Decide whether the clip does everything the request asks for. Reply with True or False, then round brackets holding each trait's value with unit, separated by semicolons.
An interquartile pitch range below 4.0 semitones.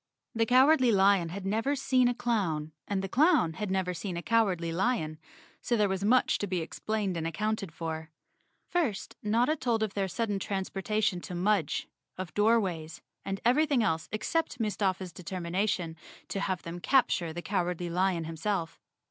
False (4.4 semitones)